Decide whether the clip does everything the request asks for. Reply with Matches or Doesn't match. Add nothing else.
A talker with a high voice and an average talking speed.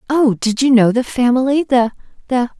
Matches